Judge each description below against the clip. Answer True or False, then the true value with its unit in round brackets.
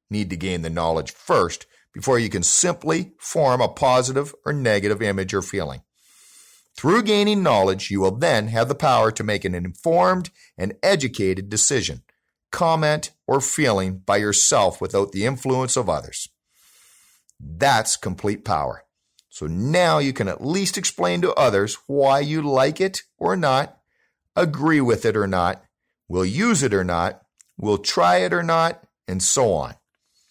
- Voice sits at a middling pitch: False (110 Hz)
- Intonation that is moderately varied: False (7.9 semitones)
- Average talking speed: True (160 wpm)